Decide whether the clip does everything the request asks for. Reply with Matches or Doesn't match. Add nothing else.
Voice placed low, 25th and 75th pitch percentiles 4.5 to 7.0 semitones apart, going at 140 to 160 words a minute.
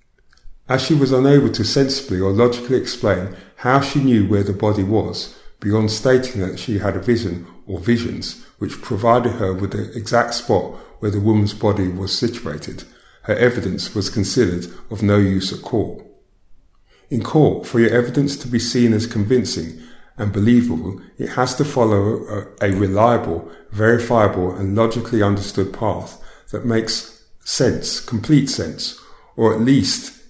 Doesn't match